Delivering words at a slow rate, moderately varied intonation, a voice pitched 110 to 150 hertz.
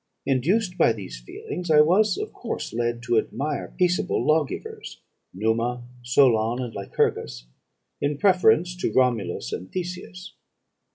No: slow, 125 wpm; wide, 7.8 semitones; low, 135 Hz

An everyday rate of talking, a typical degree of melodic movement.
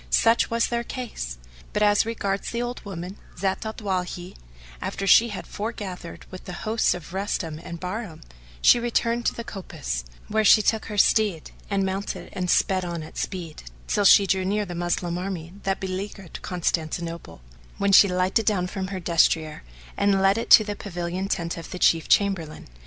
Yes: average, 180 wpm; average, 3.0 semitones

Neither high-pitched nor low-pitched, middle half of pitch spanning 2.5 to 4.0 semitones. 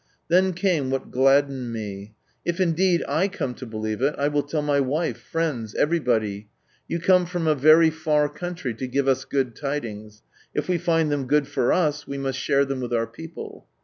No: medium, 145 Hz; average, 4.6 semitones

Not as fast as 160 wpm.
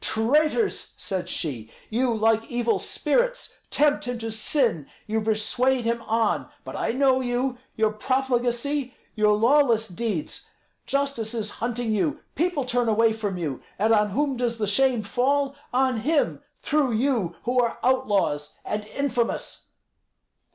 Yes: average, 145 wpm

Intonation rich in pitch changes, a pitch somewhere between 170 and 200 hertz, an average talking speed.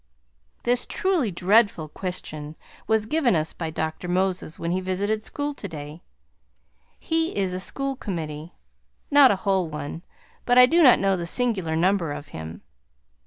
Yes: wide, 6.9 semitones; medium, 185 Hz; average, 155 wpm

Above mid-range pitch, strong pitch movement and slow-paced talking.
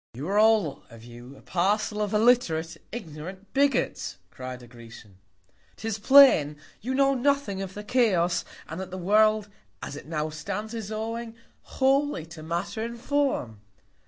No: high, 200 Hz; wide, 6.8 semitones; average, 160 wpm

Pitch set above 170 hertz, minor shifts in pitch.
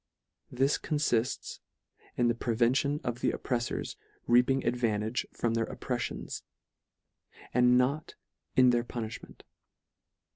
No: low, 125 Hz; narrow, 1.4 semitones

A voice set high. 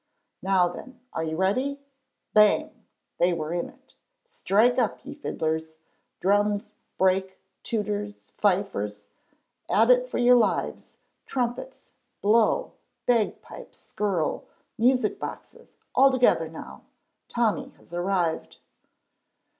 Yes: high, 205 Hz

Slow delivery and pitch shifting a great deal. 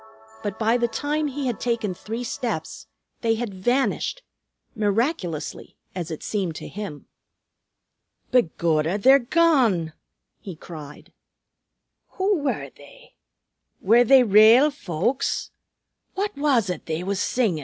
Yes: slow, 120 wpm; wide, 6.7 semitones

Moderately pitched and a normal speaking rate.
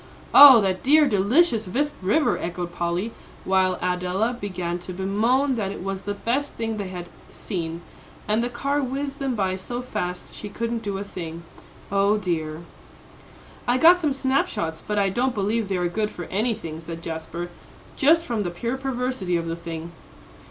No: high, 205 Hz; average, 180 wpm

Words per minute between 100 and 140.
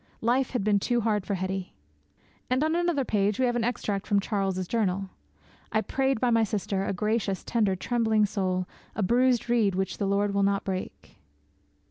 No: average, 185 wpm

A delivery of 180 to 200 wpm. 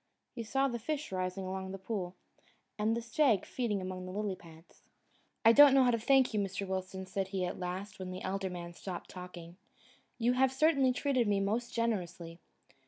Yes: average, 195 wpm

